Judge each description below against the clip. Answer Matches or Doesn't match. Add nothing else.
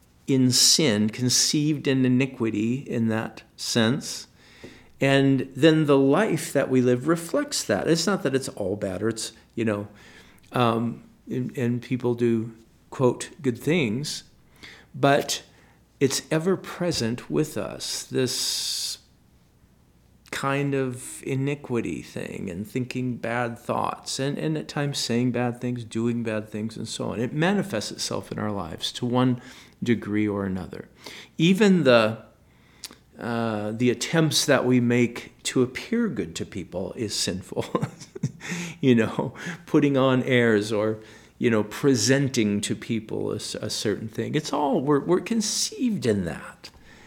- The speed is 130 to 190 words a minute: Matches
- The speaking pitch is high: Doesn't match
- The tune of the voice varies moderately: Matches